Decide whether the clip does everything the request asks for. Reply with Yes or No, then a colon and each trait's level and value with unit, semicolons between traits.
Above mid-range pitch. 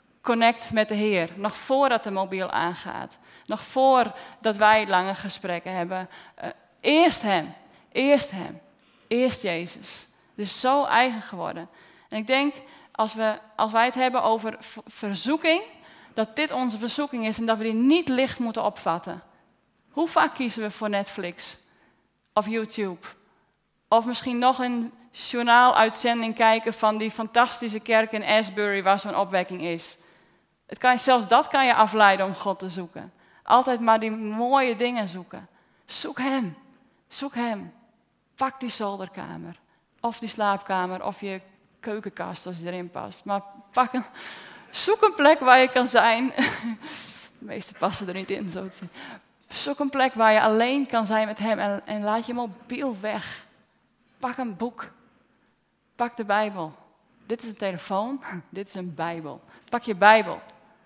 Yes: high, 225 Hz